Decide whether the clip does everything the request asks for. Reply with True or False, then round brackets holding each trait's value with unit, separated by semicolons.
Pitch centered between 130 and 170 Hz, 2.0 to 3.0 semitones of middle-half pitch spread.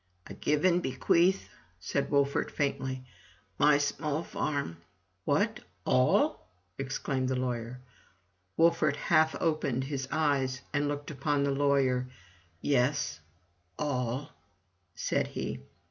True (140 Hz; 2.5 semitones)